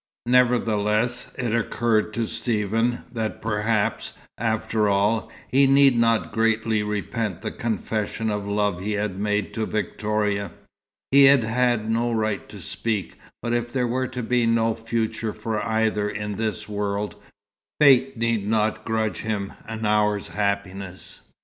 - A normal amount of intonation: No, narrow, 1.9 semitones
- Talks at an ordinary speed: Yes, average, 145 wpm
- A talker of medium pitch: No, low, 110 Hz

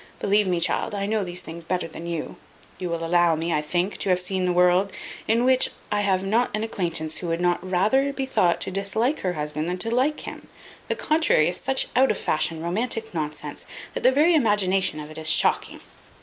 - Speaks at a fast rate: Yes, fast, 220 wpm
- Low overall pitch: No, medium, 185 Hz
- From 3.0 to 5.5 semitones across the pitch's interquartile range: Yes, average, 4.5 semitones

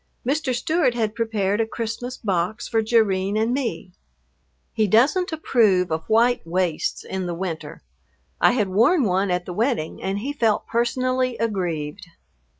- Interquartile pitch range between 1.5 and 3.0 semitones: No, average, 4.7 semitones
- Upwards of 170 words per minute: No, average, 150 wpm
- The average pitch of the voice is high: Yes, high, 220 Hz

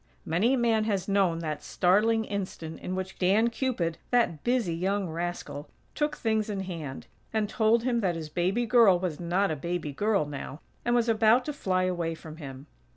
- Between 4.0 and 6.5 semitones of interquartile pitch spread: Yes, average, 5.0 semitones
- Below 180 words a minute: No, average, 190 wpm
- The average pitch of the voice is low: No, high, 190 Hz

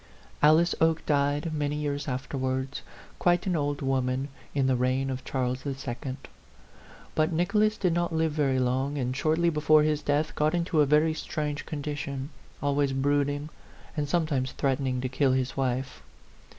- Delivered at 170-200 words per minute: No, average, 155 wpm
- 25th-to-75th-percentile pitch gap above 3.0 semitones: No, average, 2.7 semitones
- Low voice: No, medium, 145 Hz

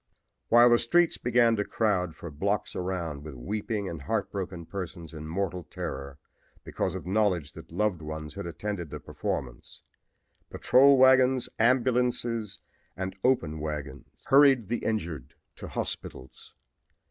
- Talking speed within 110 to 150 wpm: Yes, slow, 135 wpm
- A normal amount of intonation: No, wide, 6.7 semitones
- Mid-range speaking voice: No, low, 100 Hz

